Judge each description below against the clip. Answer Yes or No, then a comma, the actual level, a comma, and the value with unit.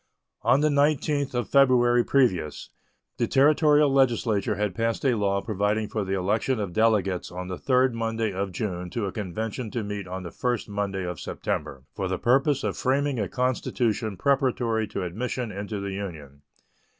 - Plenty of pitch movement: No, average, 4.6 semitones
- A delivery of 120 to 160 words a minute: No, average, 175 wpm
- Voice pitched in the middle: No, low, 110 Hz